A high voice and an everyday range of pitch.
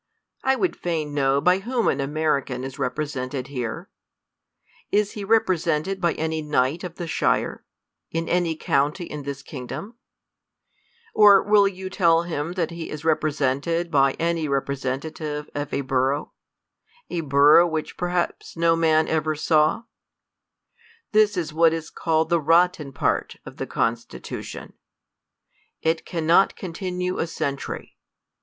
No: medium, 160 Hz; average, 3.5 semitones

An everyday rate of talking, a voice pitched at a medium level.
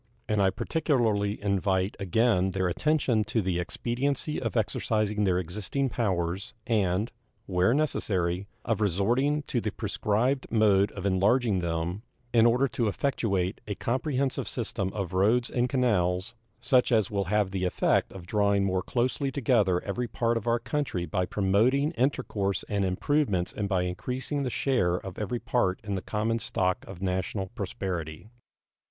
No: average, 155 wpm; low, 105 Hz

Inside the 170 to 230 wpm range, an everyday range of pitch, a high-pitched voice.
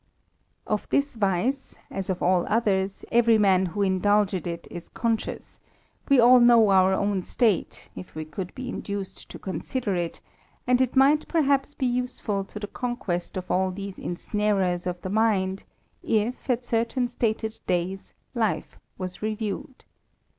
No: average, 150 wpm; average, 4.3 semitones; high, 205 Hz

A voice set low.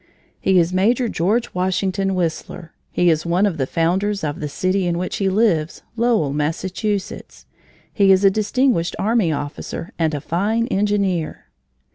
No: medium, 185 Hz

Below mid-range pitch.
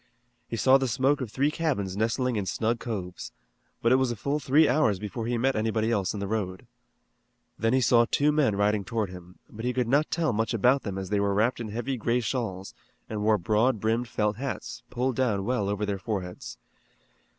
Yes: low, 115 Hz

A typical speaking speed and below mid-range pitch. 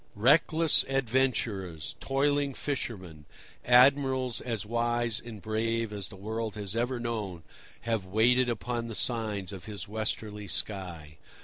No: slow, 125 wpm; low, 115 Hz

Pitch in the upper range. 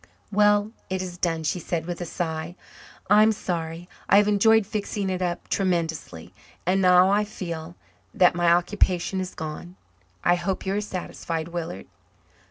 No: medium, 180 Hz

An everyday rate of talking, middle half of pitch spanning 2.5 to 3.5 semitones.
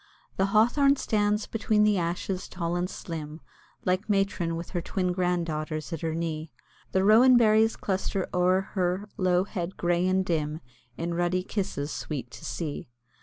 Yes: average, 165 wpm; average, 3.1 semitones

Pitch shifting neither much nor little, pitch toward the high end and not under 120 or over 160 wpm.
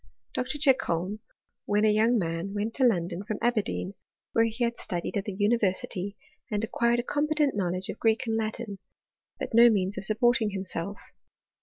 No: average, 3.4 semitones; high, 215 Hz; average, 175 wpm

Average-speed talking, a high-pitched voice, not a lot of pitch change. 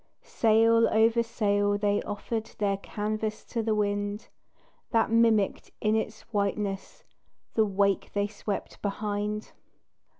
No: slow, 120 wpm; high, 210 Hz; narrow, 1.5 semitones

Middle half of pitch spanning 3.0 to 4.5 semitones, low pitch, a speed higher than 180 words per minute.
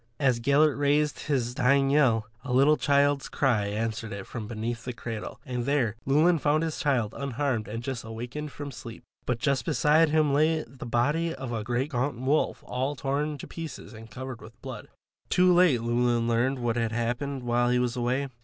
Yes: average, 3.5 semitones; low, 130 Hz; average, 190 wpm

